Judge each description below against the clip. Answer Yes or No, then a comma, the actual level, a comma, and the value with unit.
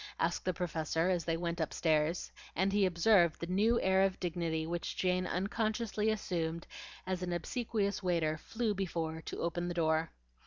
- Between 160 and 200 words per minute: Yes, average, 165 wpm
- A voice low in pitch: No, medium, 175 Hz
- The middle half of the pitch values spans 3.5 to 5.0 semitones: No, average, 2.9 semitones